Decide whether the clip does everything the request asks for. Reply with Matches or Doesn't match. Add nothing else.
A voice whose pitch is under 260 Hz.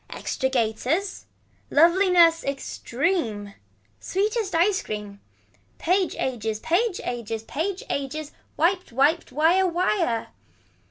Doesn't match